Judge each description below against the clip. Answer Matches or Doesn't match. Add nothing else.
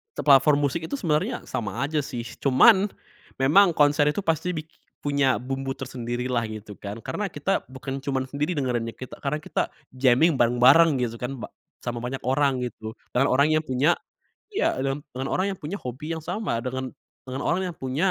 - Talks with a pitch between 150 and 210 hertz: Doesn't match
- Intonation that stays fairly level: Doesn't match